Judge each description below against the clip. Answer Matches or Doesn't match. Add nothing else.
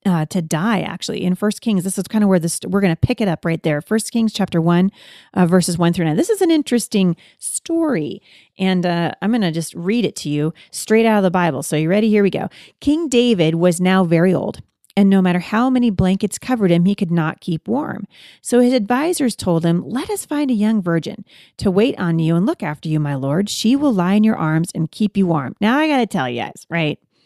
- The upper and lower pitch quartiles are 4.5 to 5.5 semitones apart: Matches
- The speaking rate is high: Matches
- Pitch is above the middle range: Matches